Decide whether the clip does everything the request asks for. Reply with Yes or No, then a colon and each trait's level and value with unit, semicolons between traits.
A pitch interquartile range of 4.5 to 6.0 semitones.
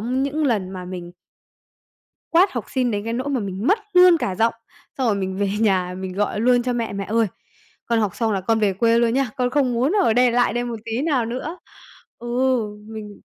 No: average, 3.7 semitones